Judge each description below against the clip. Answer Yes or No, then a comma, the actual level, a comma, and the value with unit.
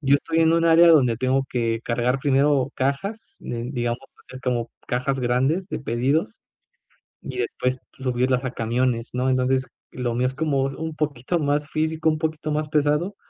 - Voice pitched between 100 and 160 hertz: Yes, low, 135 Hz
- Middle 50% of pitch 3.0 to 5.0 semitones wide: Yes, average, 3.5 semitones